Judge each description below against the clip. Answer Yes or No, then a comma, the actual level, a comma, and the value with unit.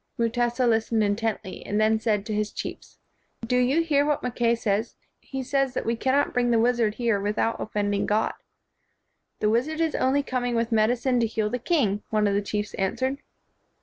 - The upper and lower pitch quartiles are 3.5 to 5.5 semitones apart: No, average, 3.0 semitones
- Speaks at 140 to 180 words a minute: No, average, 200 wpm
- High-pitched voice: Yes, high, 230 Hz